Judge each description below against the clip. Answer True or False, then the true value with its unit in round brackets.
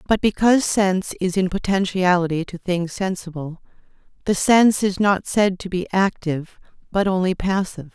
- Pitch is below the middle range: False (185 Hz)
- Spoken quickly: False (150 wpm)